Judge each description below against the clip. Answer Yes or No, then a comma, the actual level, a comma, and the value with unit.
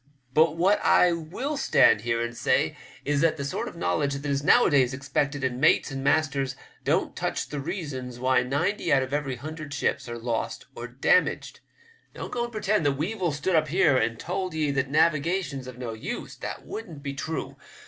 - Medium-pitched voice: Yes, medium, 145 Hz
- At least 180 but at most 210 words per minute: Yes, average, 195 wpm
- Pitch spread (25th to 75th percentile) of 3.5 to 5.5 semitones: Yes, average, 4.1 semitones